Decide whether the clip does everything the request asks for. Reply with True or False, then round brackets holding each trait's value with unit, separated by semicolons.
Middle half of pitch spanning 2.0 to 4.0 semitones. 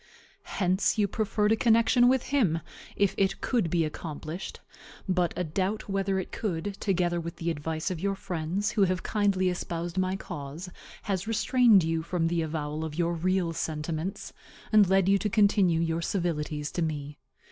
True (3.5 semitones)